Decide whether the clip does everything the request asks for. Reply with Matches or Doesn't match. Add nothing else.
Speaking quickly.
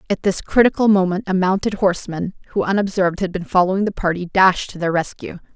Doesn't match